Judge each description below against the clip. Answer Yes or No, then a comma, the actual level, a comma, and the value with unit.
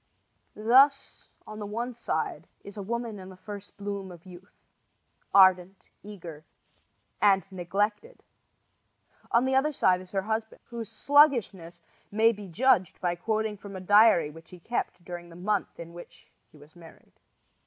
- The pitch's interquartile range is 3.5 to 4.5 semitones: Yes, average, 3.8 semitones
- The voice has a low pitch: No, high, 200 Hz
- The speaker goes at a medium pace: Yes, average, 155 wpm